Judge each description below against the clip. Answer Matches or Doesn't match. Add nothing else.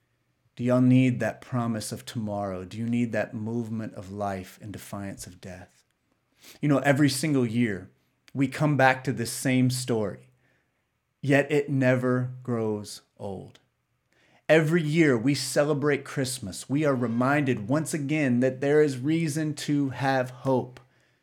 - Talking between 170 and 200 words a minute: Doesn't match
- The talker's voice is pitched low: Matches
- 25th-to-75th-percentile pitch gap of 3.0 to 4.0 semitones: Matches